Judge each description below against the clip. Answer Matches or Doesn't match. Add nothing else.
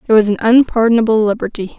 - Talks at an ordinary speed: Matches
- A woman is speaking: Matches